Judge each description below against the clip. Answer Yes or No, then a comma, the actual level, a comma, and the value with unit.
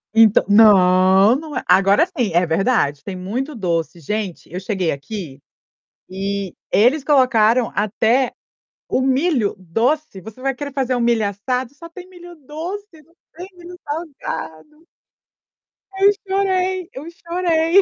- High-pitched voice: Yes, very high, 250 Hz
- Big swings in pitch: Yes, wide, 8.3 semitones